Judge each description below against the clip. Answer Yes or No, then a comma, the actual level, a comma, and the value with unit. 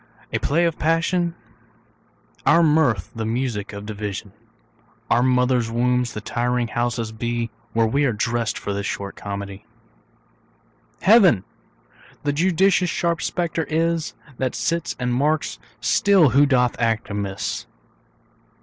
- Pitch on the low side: Yes, low, 125 Hz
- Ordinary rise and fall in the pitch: No, wide, 6.4 semitones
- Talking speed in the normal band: No, slow, 130 wpm